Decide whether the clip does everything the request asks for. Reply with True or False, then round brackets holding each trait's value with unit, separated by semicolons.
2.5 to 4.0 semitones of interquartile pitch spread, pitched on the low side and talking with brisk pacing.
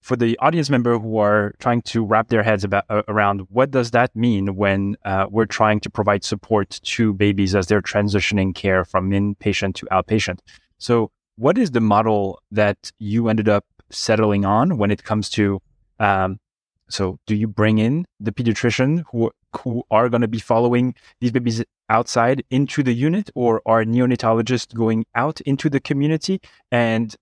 False (2.8 semitones; 110 Hz; 175 wpm)